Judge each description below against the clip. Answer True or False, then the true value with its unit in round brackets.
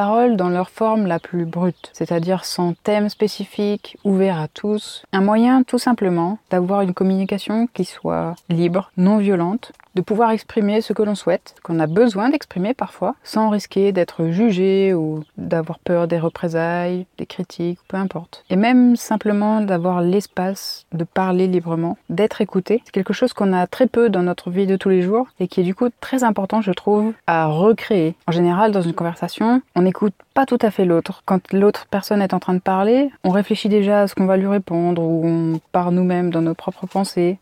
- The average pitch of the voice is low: False (190 Hz)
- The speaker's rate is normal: True (195 wpm)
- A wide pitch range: False (3.3 semitones)